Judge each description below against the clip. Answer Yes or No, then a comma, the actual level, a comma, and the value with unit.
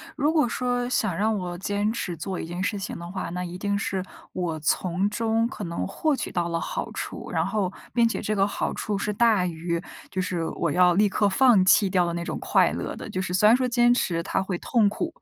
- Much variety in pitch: No, average, 3.8 semitones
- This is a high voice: Yes, high, 195 Hz